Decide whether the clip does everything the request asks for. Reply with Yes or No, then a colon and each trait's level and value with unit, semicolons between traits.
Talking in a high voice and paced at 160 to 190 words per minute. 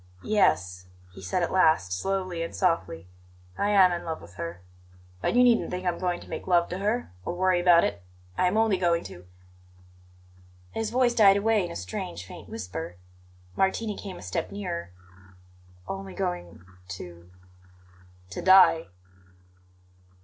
No: medium, 170 Hz; average, 165 wpm